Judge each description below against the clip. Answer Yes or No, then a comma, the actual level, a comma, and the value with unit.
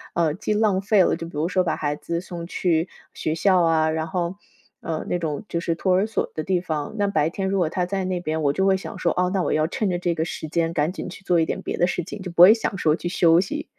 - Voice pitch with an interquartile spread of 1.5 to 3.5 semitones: Yes, average, 2.7 semitones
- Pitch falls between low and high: Yes, medium, 175 Hz